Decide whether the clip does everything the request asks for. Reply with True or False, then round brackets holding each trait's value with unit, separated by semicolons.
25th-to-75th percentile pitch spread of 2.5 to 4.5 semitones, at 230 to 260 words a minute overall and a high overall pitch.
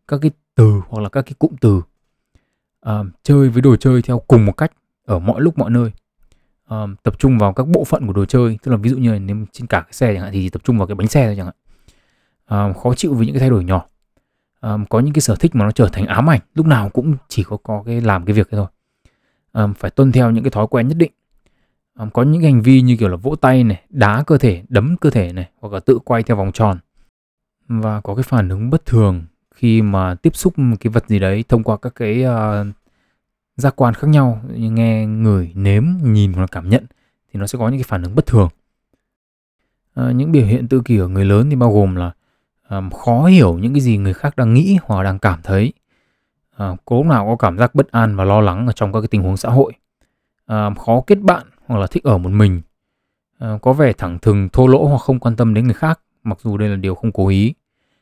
False (4.2 semitones; 250 wpm; 115 Hz)